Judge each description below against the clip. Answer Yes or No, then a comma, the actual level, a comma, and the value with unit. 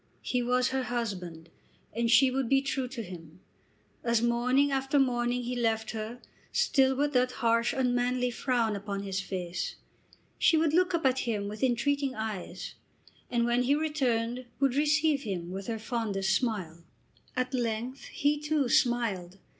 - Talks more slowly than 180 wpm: Yes, average, 160 wpm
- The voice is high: Yes, high, 245 Hz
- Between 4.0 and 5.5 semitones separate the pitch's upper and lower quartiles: No, average, 3.5 semitones